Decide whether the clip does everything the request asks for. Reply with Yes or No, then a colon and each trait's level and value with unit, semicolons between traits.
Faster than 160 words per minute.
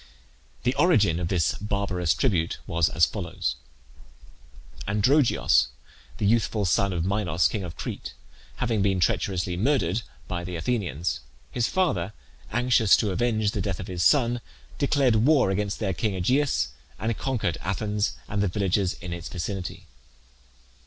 No: average, 145 wpm